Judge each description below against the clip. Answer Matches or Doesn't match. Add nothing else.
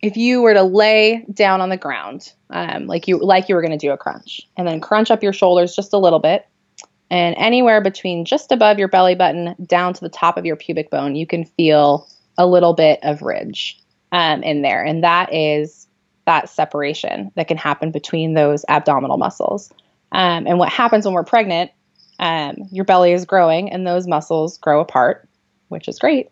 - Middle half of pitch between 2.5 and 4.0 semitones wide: Matches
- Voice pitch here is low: Doesn't match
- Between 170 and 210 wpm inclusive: Matches